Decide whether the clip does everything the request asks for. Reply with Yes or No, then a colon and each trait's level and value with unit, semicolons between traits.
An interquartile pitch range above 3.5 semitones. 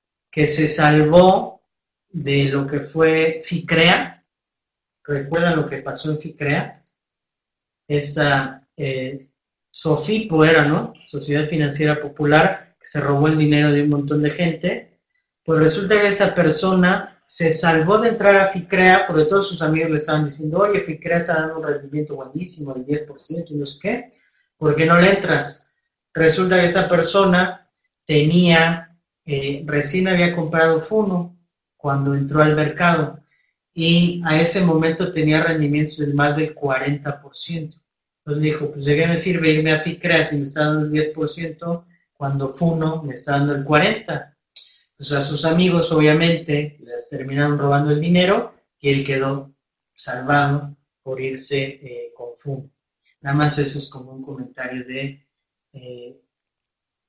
No: average, 2.8 semitones